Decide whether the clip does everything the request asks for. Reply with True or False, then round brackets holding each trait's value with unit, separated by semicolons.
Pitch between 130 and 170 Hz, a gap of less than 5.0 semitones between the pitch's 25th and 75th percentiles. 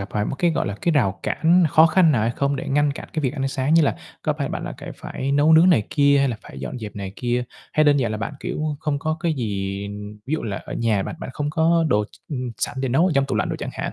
False (140 Hz; 5.3 semitones)